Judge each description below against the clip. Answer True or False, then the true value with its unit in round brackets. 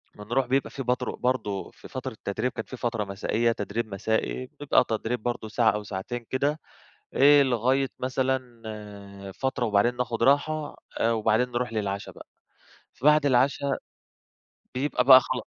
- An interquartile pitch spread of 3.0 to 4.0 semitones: True (3.5 semitones)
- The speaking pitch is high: False (120 Hz)